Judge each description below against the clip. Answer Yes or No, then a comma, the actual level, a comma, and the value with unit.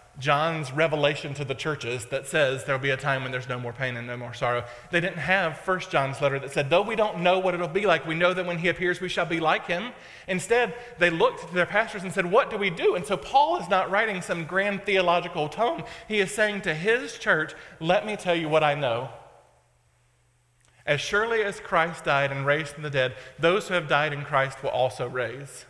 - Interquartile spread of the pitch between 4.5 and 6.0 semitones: Yes, wide, 5.6 semitones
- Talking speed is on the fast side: Yes, fast, 235 wpm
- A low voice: No, medium, 165 Hz